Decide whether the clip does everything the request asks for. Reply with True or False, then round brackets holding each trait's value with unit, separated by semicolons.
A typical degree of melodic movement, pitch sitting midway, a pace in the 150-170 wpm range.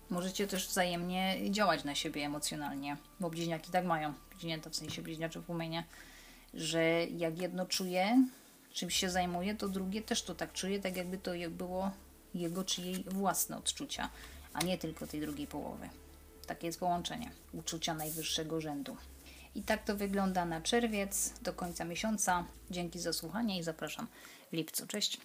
True (3.0 semitones; 180 Hz; 160 wpm)